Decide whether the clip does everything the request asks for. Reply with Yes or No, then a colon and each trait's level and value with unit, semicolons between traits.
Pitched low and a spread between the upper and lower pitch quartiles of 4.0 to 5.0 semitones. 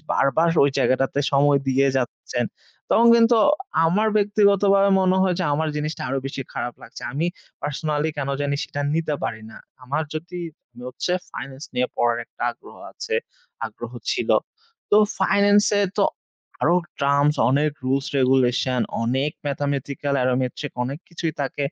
No: medium, 145 Hz; average, 4.4 semitones